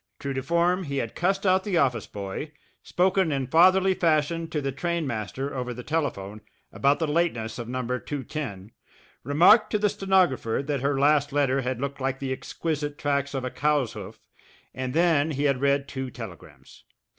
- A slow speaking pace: No, average, 180 wpm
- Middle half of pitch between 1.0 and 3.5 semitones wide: No, average, 4.2 semitones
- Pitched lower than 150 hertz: Yes, medium, 140 Hz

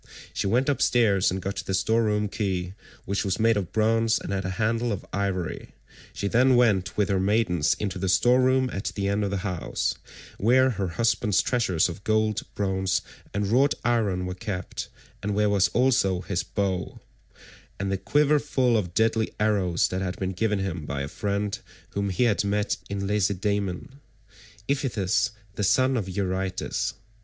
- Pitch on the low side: Yes, low, 100 Hz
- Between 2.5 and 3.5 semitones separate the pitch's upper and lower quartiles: Yes, average, 3.1 semitones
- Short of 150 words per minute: No, average, 175 wpm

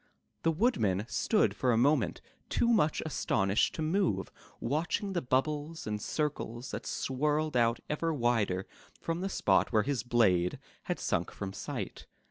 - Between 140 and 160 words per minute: Yes, average, 155 wpm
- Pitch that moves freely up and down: Yes, wide, 6.2 semitones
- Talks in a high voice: No, low, 135 Hz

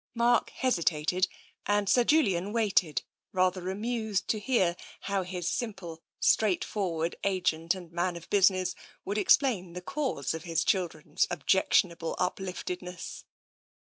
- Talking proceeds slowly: Yes, slow, 125 wpm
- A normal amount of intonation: Yes, average, 3.2 semitones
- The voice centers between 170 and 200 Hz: Yes, medium, 185 Hz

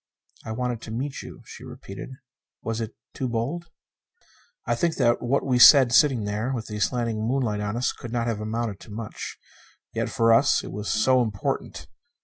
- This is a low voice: Yes, low, 115 Hz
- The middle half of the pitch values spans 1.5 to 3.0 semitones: Yes, narrow, 2.6 semitones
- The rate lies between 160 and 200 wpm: Yes, average, 185 wpm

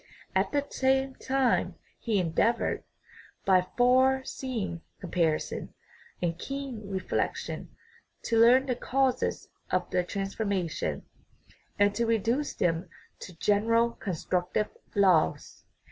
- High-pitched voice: Yes, high, 220 Hz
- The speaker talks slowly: Yes, slow, 110 wpm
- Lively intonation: Yes, wide, 5.8 semitones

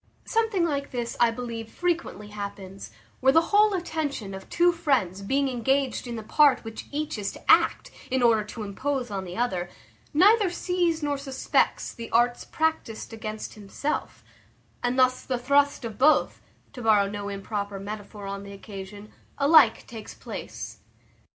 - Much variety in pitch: Yes, wide, 5.7 semitones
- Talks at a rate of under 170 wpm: Yes, average, 160 wpm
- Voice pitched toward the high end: Yes, high, 240 Hz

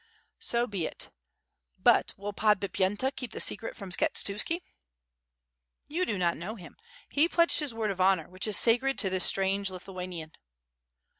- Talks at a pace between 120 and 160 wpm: Yes, average, 155 wpm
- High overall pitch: Yes, high, 200 Hz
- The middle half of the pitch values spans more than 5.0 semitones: No, average, 4.1 semitones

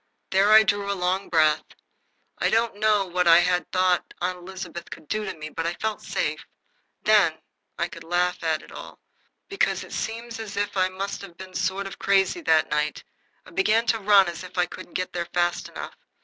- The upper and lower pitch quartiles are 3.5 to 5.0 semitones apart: No, average, 2.8 semitones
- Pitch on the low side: No, medium, 185 Hz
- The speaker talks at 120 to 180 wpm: No, fast, 205 wpm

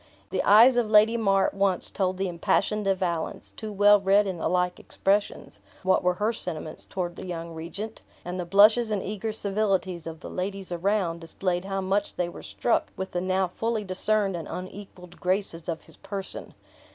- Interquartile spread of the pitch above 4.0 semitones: No, narrow, 2.5 semitones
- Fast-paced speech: No, average, 190 wpm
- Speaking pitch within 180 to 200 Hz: Yes, high, 190 Hz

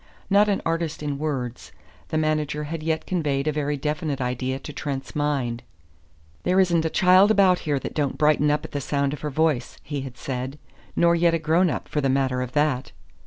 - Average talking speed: No, fast, 210 wpm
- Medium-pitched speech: Yes, medium, 150 Hz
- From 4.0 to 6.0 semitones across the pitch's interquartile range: No, average, 3.0 semitones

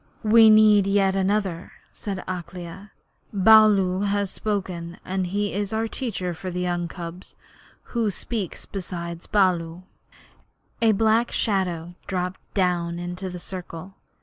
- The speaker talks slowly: Yes, slow, 125 wpm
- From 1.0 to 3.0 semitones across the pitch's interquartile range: Yes, average, 2.7 semitones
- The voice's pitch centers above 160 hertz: Yes, high, 190 Hz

